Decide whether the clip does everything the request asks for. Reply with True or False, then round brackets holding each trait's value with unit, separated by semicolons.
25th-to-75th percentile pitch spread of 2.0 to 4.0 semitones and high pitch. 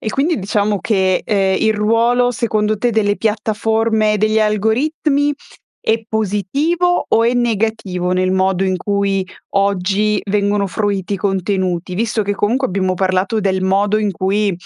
True (2.6 semitones; 210 Hz)